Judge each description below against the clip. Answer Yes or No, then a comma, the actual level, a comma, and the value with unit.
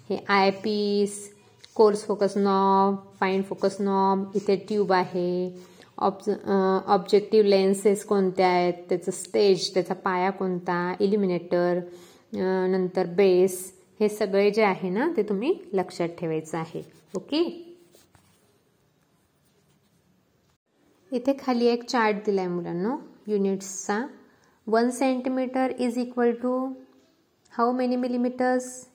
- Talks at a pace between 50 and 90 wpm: No, average, 110 wpm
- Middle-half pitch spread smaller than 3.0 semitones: No, average, 4.0 semitones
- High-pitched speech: Yes, high, 200 Hz